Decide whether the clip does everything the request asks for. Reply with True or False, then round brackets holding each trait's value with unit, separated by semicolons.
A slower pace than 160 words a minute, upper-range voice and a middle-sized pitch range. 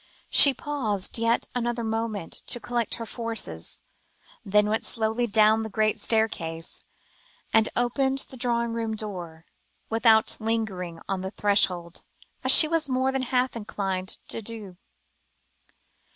True (135 wpm; 220 Hz; 3.1 semitones)